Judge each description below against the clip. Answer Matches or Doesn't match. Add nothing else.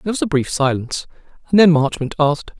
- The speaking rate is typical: Doesn't match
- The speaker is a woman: Doesn't match